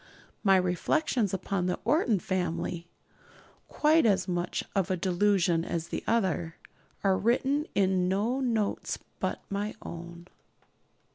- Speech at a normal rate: No, slow, 125 wpm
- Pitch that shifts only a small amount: No, average, 3.8 semitones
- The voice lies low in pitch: No, high, 190 Hz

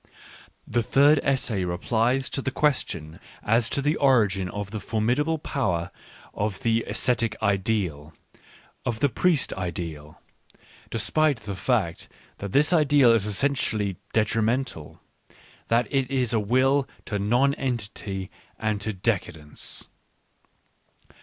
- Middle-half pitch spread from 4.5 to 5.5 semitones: Yes, average, 5.1 semitones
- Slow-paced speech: Yes, slow, 120 wpm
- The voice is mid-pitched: No, low, 115 Hz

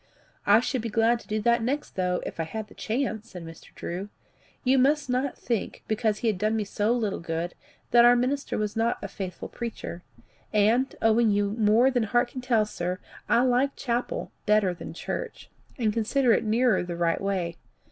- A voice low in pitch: No, high, 225 Hz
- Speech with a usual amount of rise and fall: Yes, average, 3.3 semitones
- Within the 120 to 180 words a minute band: No, average, 200 wpm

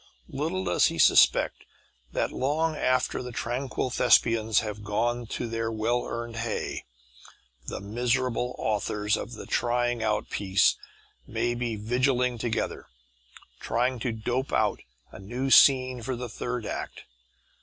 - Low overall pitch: Yes, low, 120 Hz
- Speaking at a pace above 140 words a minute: No, slow, 135 wpm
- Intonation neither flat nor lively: No, narrow, 2.2 semitones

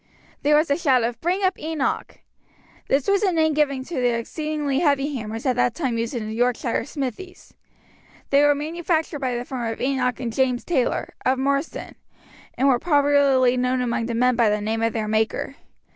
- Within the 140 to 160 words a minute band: No, average, 195 wpm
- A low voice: No, very high, 265 Hz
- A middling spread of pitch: Yes, average, 3.7 semitones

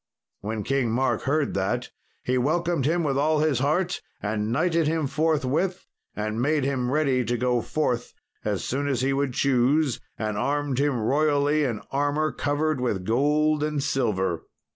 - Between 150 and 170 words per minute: Yes, average, 165 wpm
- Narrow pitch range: No, average, 3.8 semitones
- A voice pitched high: No, medium, 140 Hz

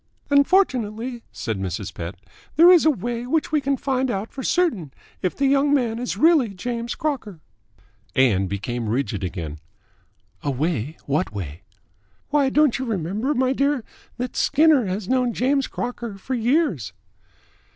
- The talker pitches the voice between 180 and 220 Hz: No, high, 235 Hz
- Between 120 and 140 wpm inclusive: No, average, 160 wpm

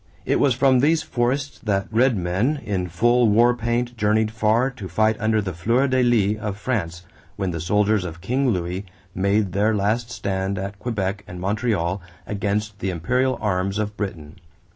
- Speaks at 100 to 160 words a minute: No, average, 175 wpm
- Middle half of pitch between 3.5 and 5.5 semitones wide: Yes, average, 3.9 semitones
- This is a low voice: Yes, low, 105 Hz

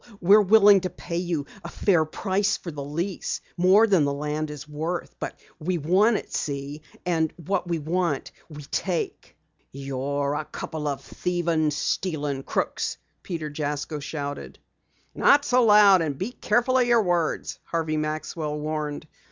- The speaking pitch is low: No, medium, 160 Hz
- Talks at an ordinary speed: Yes, average, 155 wpm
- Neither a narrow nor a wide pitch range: Yes, average, 3.9 semitones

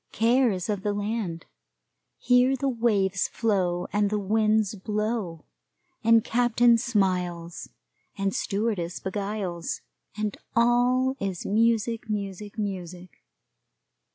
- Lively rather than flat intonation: No, average, 3.3 semitones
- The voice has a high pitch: Yes, high, 210 Hz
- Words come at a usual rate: No, slow, 105 wpm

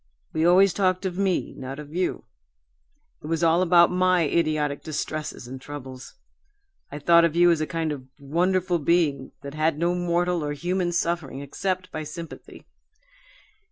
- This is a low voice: No, medium, 165 Hz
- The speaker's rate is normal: Yes, average, 160 wpm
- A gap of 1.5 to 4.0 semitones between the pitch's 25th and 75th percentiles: Yes, average, 3.1 semitones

